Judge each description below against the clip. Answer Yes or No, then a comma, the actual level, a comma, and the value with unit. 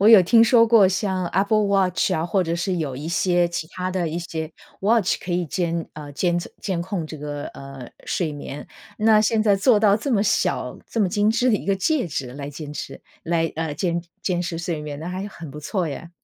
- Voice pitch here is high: No, medium, 175 Hz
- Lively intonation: No, average, 4.0 semitones